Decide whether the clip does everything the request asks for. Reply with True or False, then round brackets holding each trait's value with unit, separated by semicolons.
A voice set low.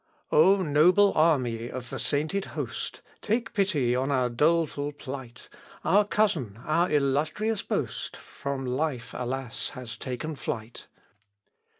False (145 Hz)